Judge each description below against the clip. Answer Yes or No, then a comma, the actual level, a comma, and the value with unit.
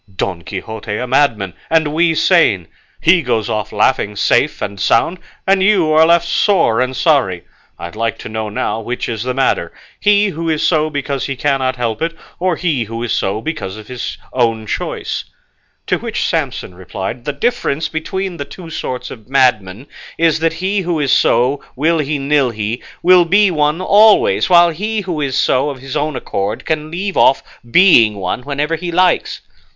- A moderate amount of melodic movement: No, wide, 6.7 semitones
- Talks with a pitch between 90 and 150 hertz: Yes, medium, 140 Hz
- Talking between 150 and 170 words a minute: No, average, 185 wpm